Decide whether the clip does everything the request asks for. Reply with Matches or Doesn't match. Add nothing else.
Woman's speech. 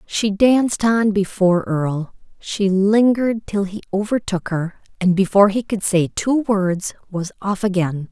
Matches